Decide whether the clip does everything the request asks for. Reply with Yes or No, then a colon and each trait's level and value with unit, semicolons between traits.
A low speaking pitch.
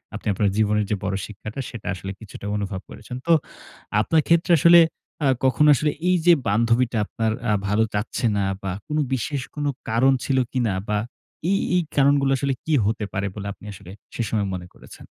Yes: low, 115 Hz